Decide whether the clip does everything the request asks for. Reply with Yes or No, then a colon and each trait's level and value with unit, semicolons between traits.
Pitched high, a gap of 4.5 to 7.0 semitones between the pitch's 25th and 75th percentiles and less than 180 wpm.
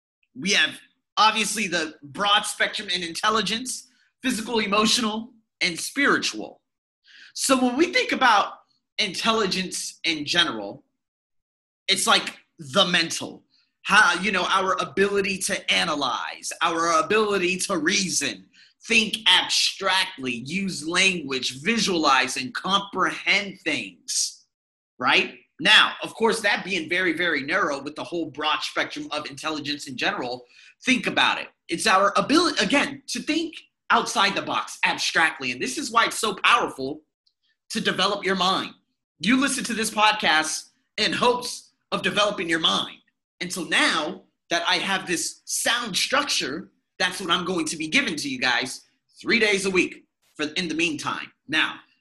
Yes: high, 195 Hz; average, 5.1 semitones; average, 145 wpm